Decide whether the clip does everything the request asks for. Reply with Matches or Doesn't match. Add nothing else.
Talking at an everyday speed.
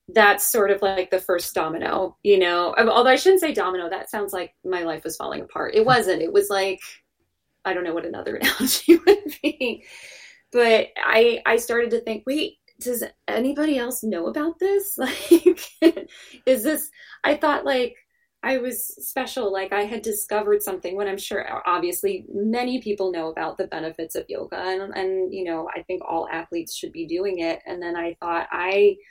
Matches